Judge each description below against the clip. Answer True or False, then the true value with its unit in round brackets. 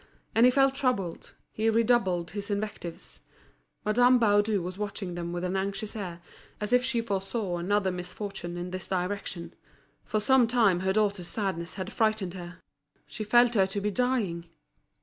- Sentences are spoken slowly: False (165 wpm)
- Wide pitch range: False (3.6 semitones)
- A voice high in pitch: True (200 Hz)